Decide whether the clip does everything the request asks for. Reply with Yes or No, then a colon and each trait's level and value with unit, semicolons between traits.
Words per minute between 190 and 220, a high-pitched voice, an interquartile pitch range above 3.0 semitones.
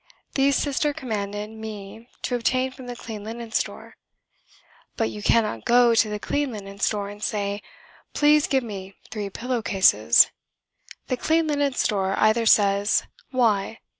No: average, 150 wpm; high, 220 Hz; average, 3.8 semitones